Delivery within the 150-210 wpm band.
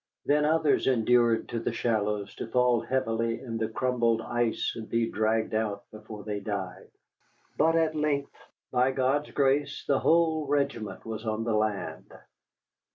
Yes: average, 155 wpm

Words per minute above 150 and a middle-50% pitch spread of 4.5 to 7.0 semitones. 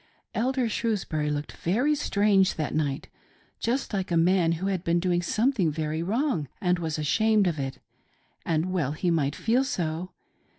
Yes: average, 165 wpm; wide, 5.4 semitones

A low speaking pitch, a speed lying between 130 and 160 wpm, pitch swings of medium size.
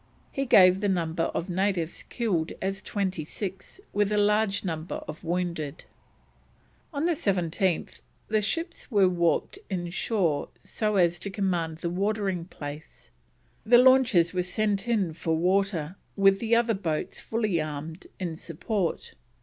No: high, 190 Hz; average, 140 wpm; average, 3.8 semitones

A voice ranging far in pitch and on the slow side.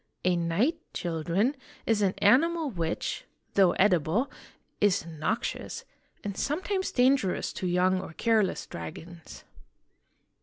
Yes: wide, 6.6 semitones; slow, 110 wpm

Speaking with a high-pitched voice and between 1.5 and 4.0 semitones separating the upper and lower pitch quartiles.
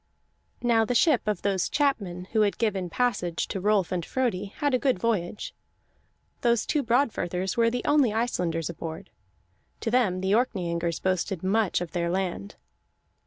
No: high, 200 Hz; average, 4.9 semitones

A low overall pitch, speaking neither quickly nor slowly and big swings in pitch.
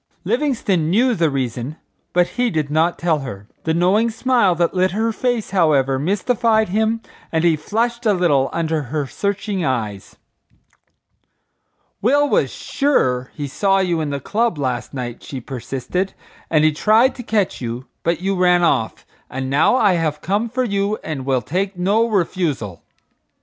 No: medium, 175 Hz; average, 165 wpm; wide, 7.1 semitones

